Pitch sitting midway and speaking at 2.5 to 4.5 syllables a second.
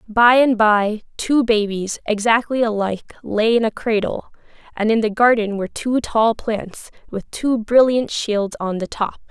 No: high, 220 Hz; 4.4 syllables/s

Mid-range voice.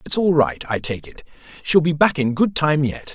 Yes: medium, 150 Hz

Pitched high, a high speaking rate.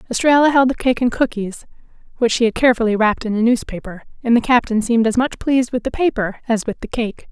Yes: high, 235 Hz; fast, 230 wpm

